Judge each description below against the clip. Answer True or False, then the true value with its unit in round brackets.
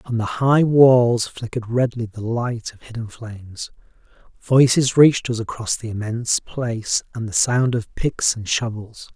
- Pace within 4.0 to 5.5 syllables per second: True (4.5 syllables/s)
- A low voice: True (120 Hz)